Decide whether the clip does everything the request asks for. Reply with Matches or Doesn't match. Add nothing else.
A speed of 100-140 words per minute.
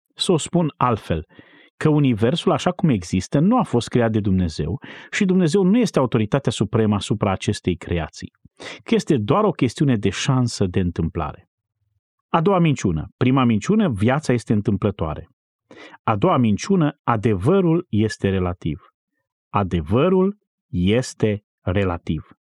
Matches